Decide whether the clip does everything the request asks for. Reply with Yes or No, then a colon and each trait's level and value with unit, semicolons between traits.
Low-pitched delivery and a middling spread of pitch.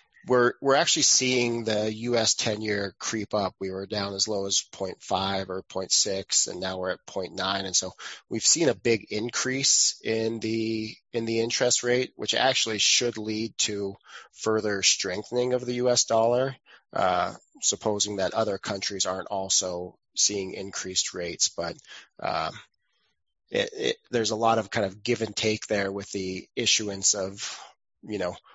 Yes: low, 110 Hz; average, 3.2 semitones